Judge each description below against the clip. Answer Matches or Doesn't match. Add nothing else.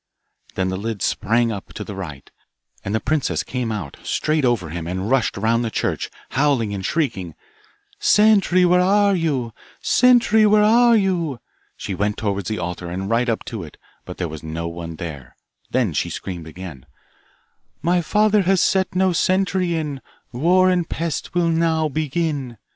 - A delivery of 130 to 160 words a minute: Doesn't match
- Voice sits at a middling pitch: Doesn't match